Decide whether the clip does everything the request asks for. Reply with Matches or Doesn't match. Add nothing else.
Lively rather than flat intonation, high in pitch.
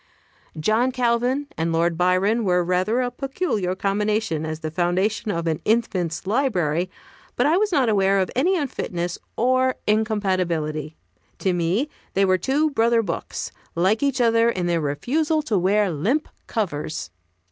Matches